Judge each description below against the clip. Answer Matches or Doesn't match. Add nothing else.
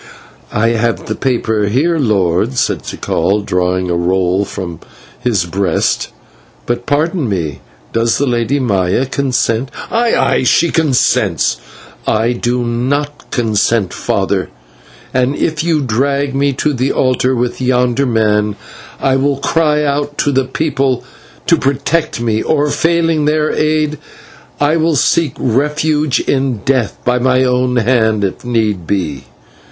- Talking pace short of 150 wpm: Matches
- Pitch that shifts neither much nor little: Matches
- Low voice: Matches